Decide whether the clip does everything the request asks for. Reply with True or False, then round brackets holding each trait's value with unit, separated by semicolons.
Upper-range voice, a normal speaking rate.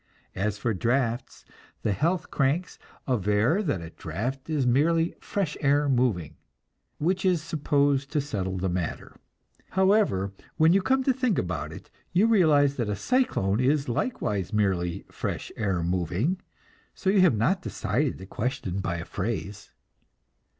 False (130 Hz; 150 wpm)